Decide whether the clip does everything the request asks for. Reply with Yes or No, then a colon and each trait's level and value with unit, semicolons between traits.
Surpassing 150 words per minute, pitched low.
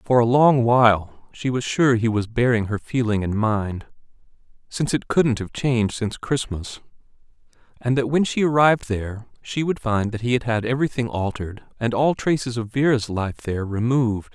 Yes: average, 185 wpm; low, 120 Hz